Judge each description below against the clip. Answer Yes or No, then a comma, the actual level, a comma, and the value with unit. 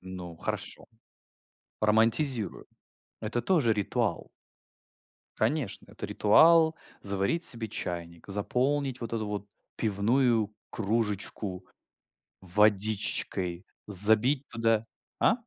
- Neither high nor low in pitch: No, low, 110 Hz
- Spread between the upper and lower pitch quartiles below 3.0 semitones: No, average, 3.3 semitones